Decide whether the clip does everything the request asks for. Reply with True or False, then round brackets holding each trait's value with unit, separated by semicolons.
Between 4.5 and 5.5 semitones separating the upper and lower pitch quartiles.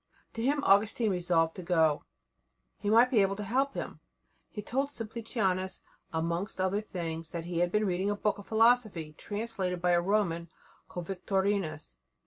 False (3.8 semitones)